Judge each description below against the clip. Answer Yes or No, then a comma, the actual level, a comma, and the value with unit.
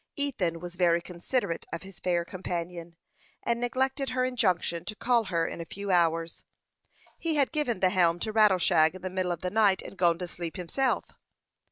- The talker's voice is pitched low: No, medium, 185 Hz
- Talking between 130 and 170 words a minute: No, average, 190 wpm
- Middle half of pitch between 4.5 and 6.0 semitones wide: Yes, average, 5.0 semitones